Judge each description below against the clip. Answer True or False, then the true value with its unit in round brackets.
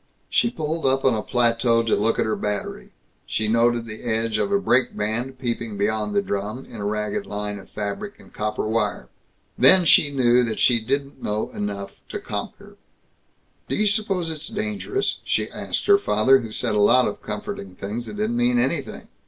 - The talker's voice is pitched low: True (120 Hz)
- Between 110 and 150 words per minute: False (195 wpm)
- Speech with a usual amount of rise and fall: False (6.8 semitones)